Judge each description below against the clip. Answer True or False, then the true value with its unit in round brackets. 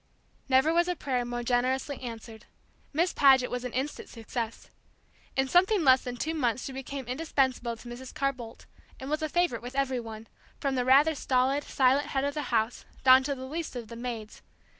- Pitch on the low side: False (260 Hz)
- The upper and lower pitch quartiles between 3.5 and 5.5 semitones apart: False (2.7 semitones)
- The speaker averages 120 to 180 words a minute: False (200 wpm)